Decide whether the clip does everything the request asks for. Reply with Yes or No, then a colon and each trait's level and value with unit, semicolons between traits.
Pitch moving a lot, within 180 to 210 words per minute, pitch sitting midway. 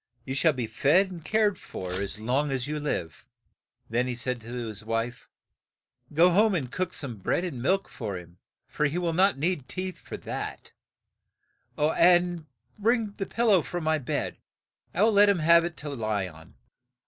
Yes: wide, 7.3 semitones; average, 185 wpm; medium, 150 Hz